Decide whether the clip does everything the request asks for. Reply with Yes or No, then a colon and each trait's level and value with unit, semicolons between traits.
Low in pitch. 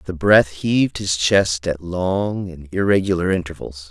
Yes: very low, 90 Hz